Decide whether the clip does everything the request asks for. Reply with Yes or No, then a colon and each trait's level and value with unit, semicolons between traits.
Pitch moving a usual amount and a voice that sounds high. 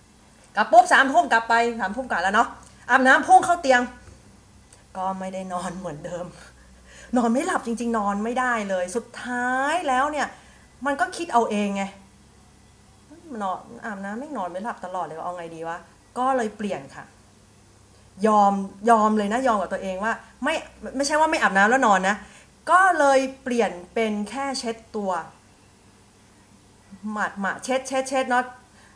No: wide, 6.2 semitones; high, 215 Hz